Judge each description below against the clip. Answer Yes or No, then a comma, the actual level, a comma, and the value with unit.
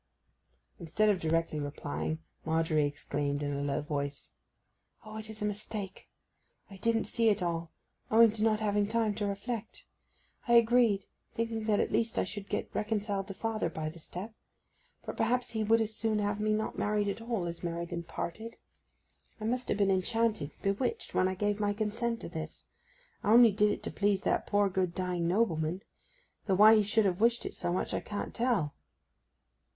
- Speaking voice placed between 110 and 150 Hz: No, high, 205 Hz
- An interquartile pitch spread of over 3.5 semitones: Yes, average, 4.2 semitones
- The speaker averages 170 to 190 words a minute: Yes, average, 180 wpm